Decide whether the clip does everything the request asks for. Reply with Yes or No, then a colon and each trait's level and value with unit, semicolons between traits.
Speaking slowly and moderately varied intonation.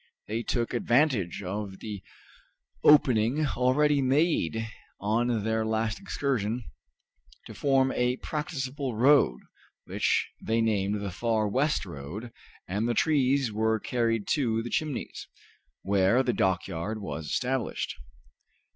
Yes: slow, 120 wpm; average, 4.2 semitones